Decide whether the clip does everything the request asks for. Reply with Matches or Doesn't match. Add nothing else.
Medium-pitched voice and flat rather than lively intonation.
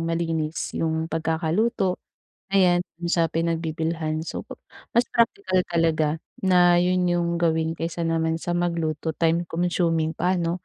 Matches